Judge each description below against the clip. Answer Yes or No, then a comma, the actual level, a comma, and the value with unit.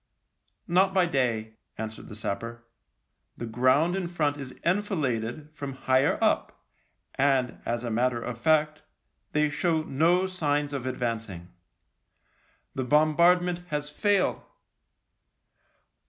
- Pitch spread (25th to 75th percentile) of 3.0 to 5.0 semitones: No, wide, 5.6 semitones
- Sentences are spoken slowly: Yes, slow, 125 wpm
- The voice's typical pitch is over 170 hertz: No, medium, 145 Hz